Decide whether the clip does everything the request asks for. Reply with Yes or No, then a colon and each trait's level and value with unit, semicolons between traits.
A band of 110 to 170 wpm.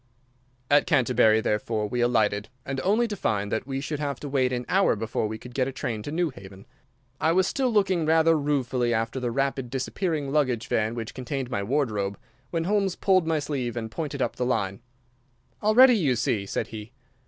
No: average, 190 wpm